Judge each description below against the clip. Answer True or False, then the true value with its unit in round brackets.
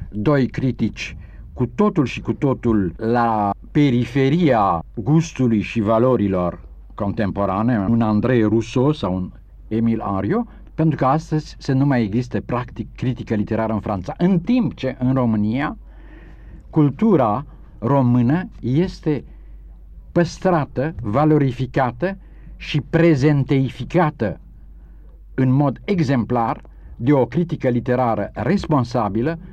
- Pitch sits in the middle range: False (125 Hz)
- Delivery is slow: True (105 wpm)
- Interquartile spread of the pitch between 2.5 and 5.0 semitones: False (5.4 semitones)